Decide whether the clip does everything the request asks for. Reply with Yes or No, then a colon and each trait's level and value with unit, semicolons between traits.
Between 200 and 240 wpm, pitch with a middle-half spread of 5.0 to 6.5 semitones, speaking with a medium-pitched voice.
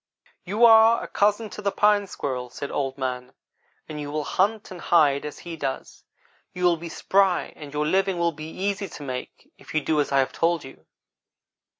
Yes: fast, 205 wpm; wide, 5.6 semitones; medium, 165 Hz